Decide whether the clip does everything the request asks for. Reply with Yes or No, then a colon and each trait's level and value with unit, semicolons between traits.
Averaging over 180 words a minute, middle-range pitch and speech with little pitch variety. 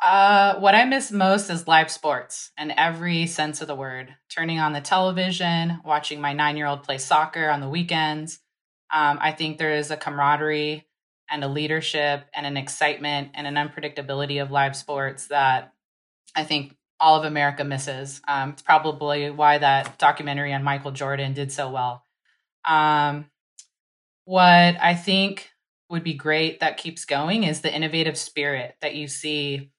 No: average, 165 wpm; medium, 150 Hz; narrow, 2.0 semitones